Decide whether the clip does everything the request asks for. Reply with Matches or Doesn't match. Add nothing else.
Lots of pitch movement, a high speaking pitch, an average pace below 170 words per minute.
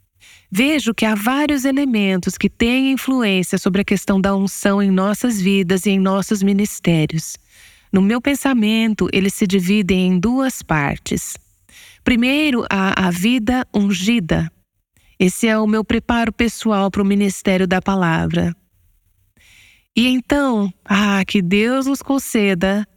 Doesn't match